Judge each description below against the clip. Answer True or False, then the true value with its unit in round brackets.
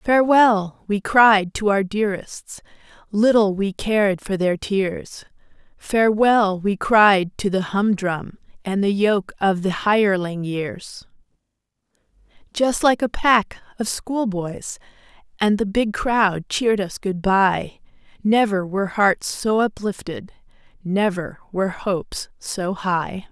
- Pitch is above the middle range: True (200 Hz)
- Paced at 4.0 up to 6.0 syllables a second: False (3.8 syllables/s)